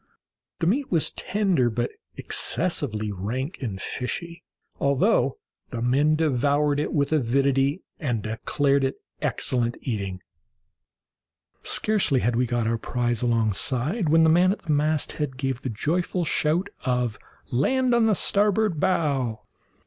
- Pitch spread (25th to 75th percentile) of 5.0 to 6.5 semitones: Yes, wide, 5.5 semitones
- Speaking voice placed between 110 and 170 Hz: Yes, medium, 140 Hz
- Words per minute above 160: No, slow, 135 wpm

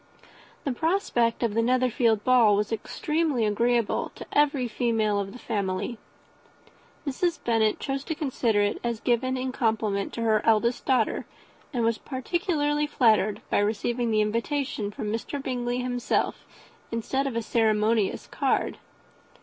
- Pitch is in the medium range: No, high, 235 Hz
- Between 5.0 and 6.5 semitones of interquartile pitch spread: No, average, 3.2 semitones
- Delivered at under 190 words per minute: Yes, average, 140 wpm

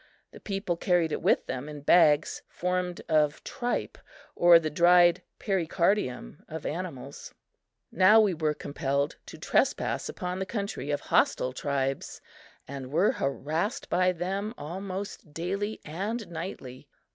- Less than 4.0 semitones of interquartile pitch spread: No, average, 4.3 semitones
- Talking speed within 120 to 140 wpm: Yes, slow, 135 wpm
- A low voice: No, medium, 170 Hz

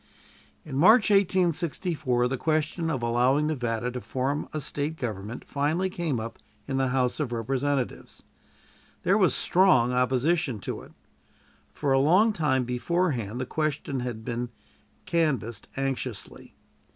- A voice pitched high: No, low, 135 Hz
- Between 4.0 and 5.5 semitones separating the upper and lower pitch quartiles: Yes, average, 4.5 semitones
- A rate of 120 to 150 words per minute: Yes, slow, 135 wpm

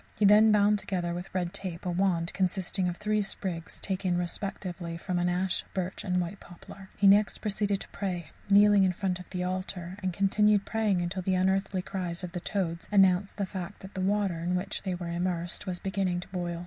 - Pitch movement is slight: Yes, narrow, 2.0 semitones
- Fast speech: Yes, fast, 210 wpm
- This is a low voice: No, medium, 185 Hz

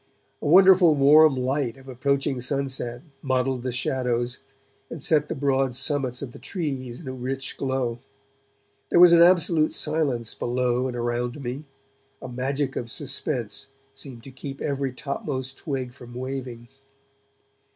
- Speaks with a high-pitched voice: No, low, 130 Hz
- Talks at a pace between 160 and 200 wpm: No, average, 145 wpm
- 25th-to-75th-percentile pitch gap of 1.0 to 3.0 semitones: Yes, narrow, 2.5 semitones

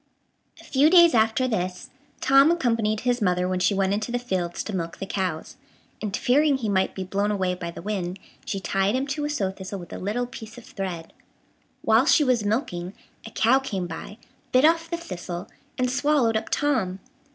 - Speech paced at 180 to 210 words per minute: Yes, average, 200 wpm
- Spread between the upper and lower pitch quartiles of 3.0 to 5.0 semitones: No, wide, 5.4 semitones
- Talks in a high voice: Yes, high, 215 Hz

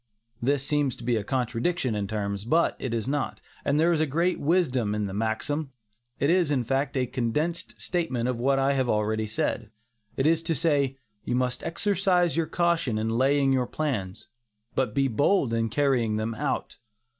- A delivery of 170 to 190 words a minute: Yes, average, 185 wpm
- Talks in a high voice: No, low, 135 Hz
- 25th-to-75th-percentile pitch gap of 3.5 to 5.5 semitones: Yes, average, 5.1 semitones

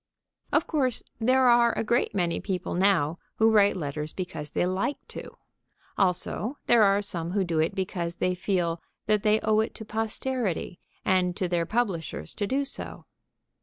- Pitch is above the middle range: Yes, high, 195 Hz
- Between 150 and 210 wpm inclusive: Yes, average, 170 wpm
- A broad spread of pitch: No, average, 4.1 semitones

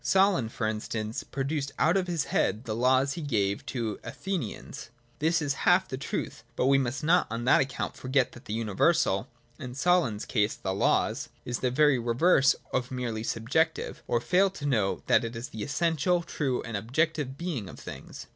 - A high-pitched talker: No, low, 130 Hz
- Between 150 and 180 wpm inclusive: No, average, 195 wpm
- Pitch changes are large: Yes, wide, 5.7 semitones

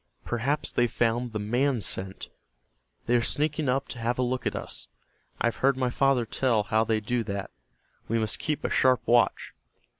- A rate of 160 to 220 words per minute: Yes, average, 190 wpm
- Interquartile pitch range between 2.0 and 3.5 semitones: Yes, narrow, 2.6 semitones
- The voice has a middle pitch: No, low, 120 Hz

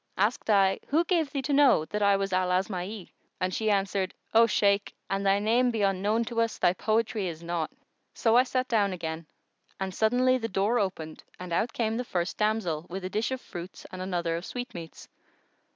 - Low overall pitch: No, high, 200 Hz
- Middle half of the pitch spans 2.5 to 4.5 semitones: Yes, average, 3.9 semitones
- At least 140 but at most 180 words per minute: No, average, 200 wpm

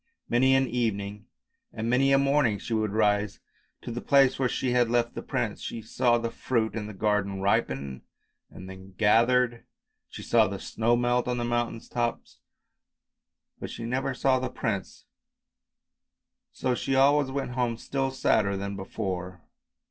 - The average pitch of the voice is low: Yes, low, 115 Hz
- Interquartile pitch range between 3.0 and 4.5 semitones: Yes, average, 3.5 semitones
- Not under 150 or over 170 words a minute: Yes, average, 165 wpm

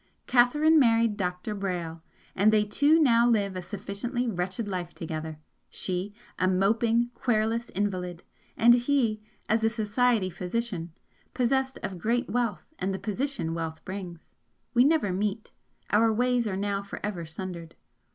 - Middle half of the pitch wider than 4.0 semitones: Yes, average, 4.4 semitones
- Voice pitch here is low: No, high, 210 Hz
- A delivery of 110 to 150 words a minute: Yes, average, 145 wpm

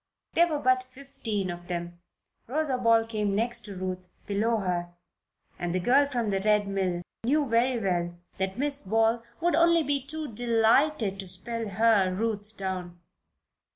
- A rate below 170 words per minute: Yes, average, 160 wpm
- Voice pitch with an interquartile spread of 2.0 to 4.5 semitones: No, average, 5.1 semitones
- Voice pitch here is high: Yes, high, 220 Hz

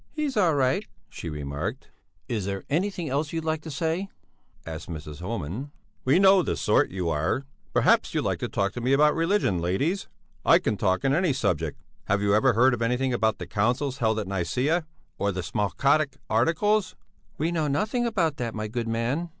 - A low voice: Yes, low, 125 Hz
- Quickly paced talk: No, average, 190 wpm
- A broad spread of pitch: Yes, wide, 8.0 semitones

